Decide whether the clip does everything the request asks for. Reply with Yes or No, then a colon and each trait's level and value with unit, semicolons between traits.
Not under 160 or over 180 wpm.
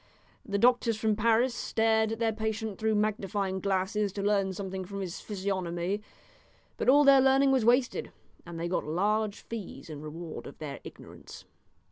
Yes: average, 165 wpm